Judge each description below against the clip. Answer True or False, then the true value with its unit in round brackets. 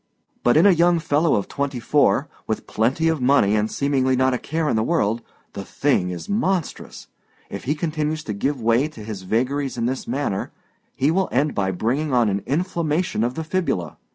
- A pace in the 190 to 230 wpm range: True (200 wpm)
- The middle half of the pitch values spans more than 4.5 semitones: True (5.6 semitones)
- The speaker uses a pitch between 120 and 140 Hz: True (135 Hz)